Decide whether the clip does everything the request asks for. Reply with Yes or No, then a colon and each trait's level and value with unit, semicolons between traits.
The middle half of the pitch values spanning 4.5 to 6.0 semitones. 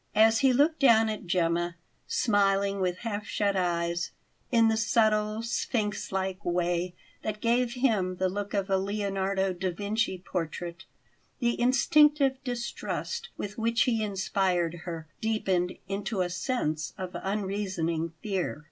No: average, 3.7 semitones